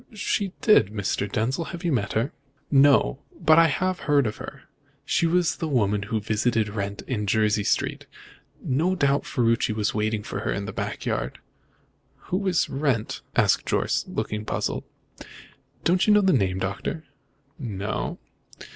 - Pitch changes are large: Yes, wide, 7.6 semitones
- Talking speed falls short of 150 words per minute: No, average, 160 wpm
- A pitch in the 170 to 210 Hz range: No, low, 120 Hz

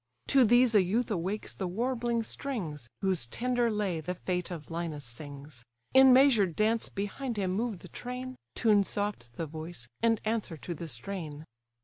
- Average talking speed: Yes, average, 165 wpm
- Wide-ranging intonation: Yes, wide, 6.1 semitones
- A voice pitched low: No, high, 200 Hz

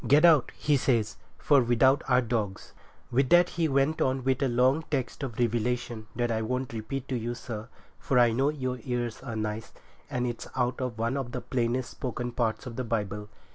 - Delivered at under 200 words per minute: No, fast, 205 wpm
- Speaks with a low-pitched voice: Yes, low, 125 Hz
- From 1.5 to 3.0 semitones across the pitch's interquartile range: Yes, narrow, 2.4 semitones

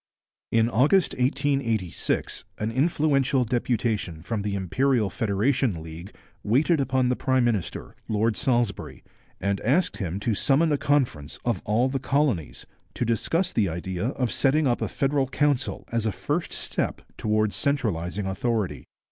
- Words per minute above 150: No, average, 145 wpm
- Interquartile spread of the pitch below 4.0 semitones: No, average, 5.1 semitones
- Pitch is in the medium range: No, low, 120 Hz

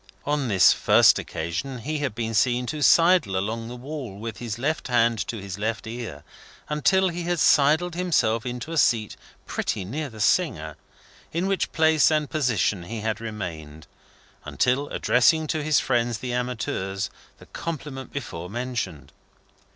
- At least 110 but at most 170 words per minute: Yes, average, 160 wpm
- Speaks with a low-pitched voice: Yes, low, 125 Hz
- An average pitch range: No, wide, 5.9 semitones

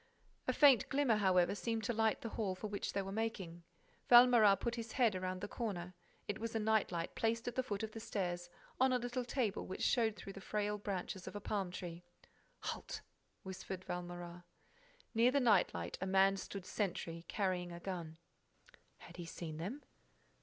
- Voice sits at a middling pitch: No, high, 200 Hz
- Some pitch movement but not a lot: Yes, average, 3.9 semitones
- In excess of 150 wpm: Yes, average, 190 wpm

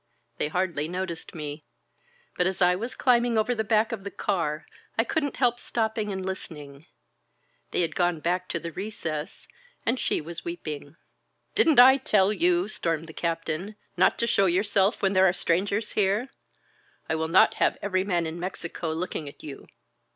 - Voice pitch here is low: No, medium, 185 Hz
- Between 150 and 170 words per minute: No, average, 180 wpm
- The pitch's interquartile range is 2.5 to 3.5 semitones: No, average, 4.4 semitones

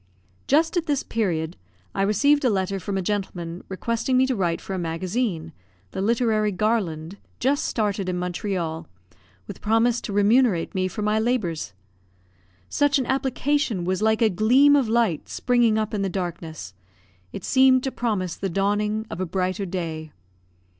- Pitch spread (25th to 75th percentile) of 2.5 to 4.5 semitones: No, average, 4.9 semitones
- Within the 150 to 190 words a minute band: Yes, average, 165 wpm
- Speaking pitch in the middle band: No, high, 205 Hz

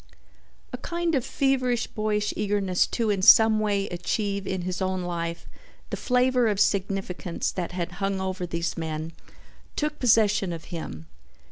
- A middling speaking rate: Yes, average, 150 wpm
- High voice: Yes, high, 195 Hz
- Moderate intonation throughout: Yes, average, 3.7 semitones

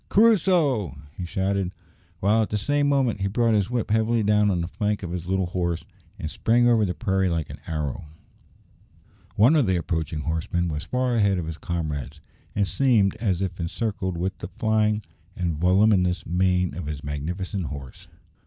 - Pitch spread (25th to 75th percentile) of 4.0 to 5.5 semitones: Yes, average, 4.3 semitones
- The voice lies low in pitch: Yes, very low, 95 Hz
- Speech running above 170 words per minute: Yes, average, 180 wpm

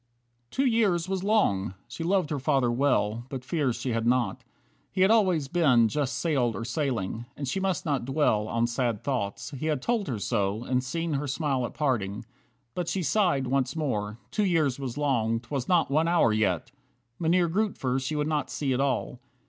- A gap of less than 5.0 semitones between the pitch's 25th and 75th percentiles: No, wide, 5.6 semitones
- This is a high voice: No, low, 135 Hz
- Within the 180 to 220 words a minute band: Yes, average, 195 wpm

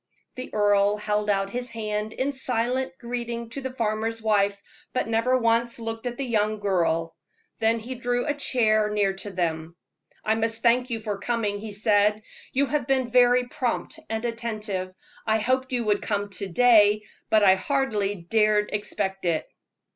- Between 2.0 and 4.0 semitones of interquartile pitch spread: Yes, average, 3.0 semitones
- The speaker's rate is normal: Yes, average, 170 wpm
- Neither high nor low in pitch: No, high, 220 Hz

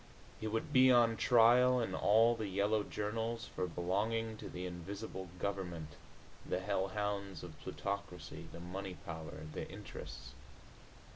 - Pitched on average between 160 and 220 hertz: No, low, 100 Hz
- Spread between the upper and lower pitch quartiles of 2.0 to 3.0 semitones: No, average, 3.9 semitones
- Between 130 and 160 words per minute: Yes, average, 140 wpm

